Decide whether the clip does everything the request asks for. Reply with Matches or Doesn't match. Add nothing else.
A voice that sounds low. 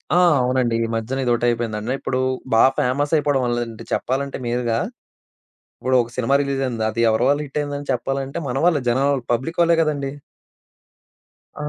Matches